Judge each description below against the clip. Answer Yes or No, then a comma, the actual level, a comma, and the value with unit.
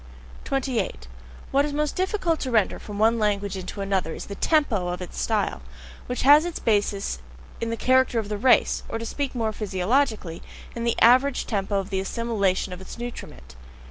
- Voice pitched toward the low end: No, high, 220 Hz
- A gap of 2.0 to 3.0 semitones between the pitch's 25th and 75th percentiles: No, average, 4.9 semitones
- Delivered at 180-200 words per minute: Yes, average, 185 wpm